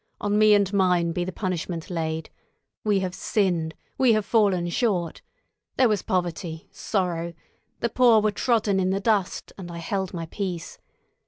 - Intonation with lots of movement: No, average, 3.4 semitones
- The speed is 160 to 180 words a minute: Yes, average, 165 wpm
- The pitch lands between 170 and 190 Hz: Yes, medium, 185 Hz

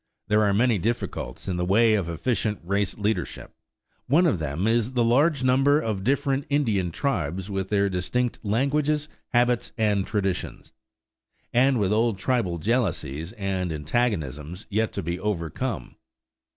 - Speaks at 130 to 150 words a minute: Yes, average, 145 wpm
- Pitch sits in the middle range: No, low, 105 Hz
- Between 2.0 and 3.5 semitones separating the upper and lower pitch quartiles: No, average, 5.1 semitones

